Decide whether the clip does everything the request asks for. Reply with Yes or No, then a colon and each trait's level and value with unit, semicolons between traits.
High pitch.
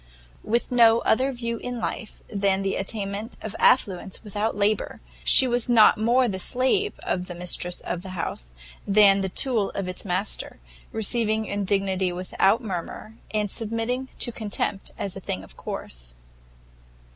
Yes: high, 205 Hz